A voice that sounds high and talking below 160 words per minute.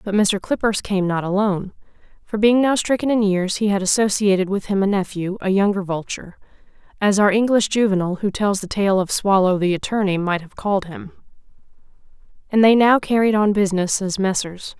No: high, 200 Hz; average, 185 wpm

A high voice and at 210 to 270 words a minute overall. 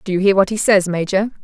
No: high, 195 Hz; fast, 295 wpm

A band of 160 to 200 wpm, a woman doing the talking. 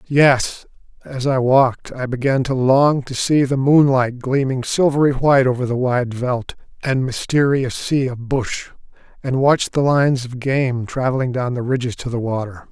No: average, 175 wpm; male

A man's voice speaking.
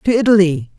No: female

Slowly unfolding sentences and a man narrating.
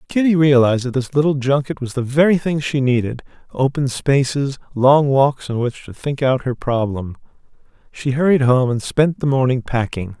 No: average, 175 wpm; male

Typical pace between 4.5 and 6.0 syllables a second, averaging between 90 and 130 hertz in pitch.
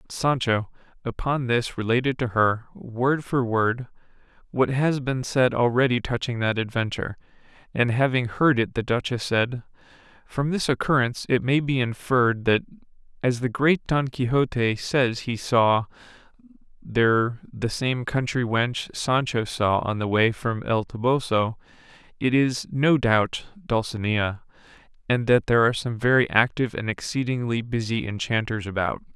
Yes: 4.6 syllables/s; low, 120 Hz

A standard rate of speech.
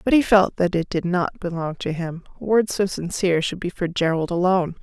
No: fast, 225 wpm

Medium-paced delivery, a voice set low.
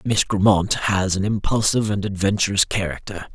Yes: average, 145 wpm; low, 100 Hz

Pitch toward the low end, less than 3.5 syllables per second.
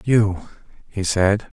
Yes: low, 100 Hz; 3.0 syllables/s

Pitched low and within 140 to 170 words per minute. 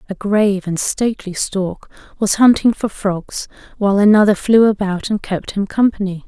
No: high, 200 Hz; average, 165 wpm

